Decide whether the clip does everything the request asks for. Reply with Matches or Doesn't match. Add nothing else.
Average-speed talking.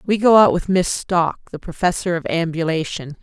Matches